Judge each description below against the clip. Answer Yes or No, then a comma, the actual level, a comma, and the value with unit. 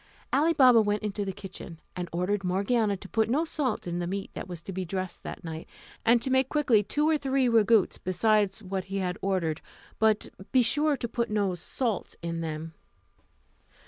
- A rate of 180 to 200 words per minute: Yes, average, 195 wpm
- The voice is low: No, high, 205 Hz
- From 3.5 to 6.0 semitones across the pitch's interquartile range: Yes, average, 4.6 semitones